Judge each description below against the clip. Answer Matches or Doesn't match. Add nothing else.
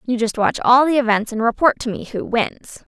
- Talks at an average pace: Doesn't match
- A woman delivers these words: Matches